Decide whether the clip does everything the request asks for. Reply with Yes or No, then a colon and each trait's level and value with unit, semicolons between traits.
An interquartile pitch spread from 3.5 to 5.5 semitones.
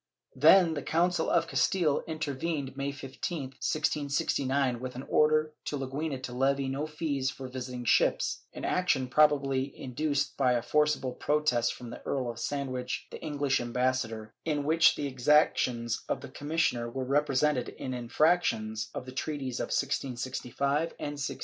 No: average, 3.0 semitones